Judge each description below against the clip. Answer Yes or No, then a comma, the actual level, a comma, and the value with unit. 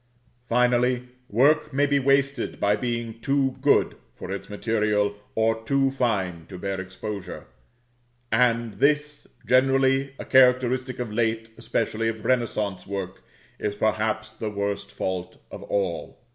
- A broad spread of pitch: No, average, 4.1 semitones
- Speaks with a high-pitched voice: No, low, 115 Hz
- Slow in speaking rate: Yes, slow, 130 wpm